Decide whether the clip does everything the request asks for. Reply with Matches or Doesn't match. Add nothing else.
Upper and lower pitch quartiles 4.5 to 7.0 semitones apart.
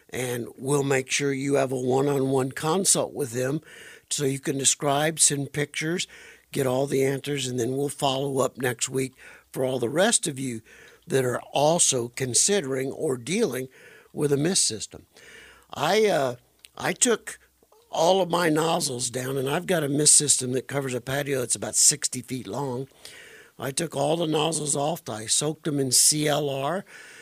Doesn't match